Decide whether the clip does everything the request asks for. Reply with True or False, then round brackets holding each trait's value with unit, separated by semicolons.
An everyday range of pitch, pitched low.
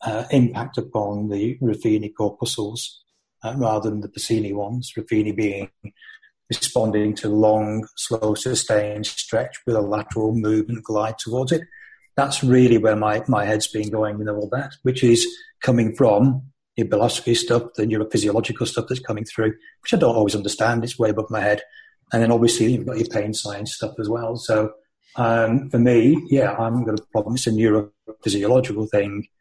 False (2.3 semitones; 110 Hz)